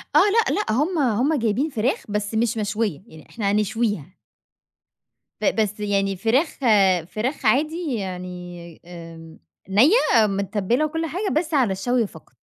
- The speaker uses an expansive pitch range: Yes, wide, 6.1 semitones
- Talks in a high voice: Yes, high, 220 Hz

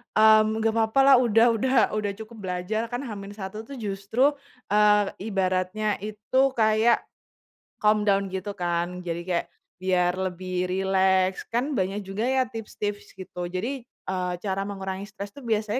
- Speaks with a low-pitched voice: No, high, 205 Hz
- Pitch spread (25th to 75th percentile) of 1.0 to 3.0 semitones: Yes, average, 2.7 semitones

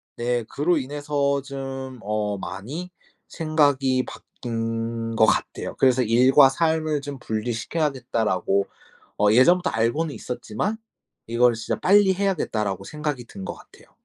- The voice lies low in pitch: Yes, low, 130 Hz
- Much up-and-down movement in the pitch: No, average, 4.6 semitones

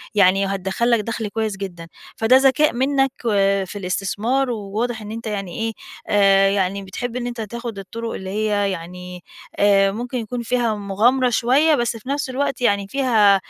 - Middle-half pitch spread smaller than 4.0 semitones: Yes, average, 3.6 semitones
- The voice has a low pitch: No, high, 215 Hz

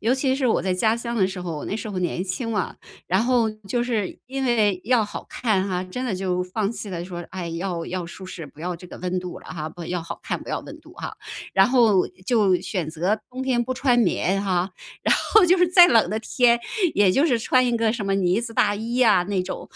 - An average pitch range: Yes, average, 4.7 semitones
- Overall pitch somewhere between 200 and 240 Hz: Yes, high, 205 Hz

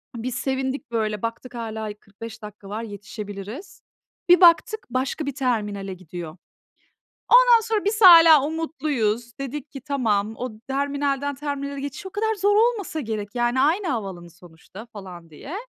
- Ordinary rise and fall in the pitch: No, wide, 6.4 semitones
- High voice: Yes, very high, 255 Hz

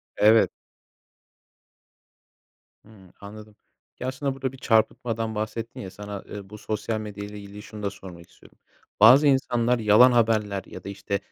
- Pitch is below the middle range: Yes, low, 110 Hz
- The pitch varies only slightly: Yes, narrow, 2.3 semitones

